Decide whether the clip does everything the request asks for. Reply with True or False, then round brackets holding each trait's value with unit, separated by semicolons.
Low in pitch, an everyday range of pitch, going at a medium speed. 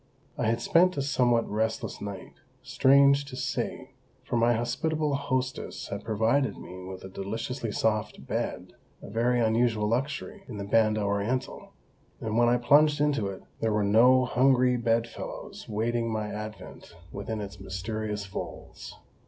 True (115 Hz; 3.3 semitones; 150 wpm)